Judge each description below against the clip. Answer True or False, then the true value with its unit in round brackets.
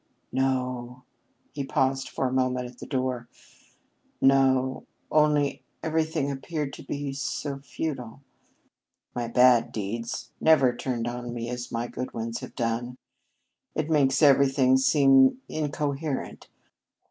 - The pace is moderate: False (125 wpm)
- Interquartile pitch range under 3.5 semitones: True (2.4 semitones)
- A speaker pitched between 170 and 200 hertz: False (130 Hz)